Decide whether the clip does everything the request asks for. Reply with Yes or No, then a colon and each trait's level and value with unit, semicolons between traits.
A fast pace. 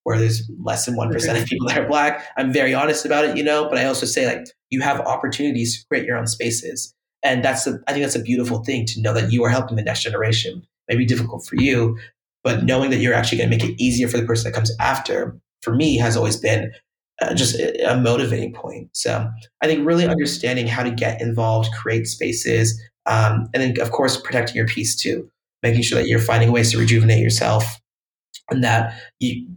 Yes: fast, 225 wpm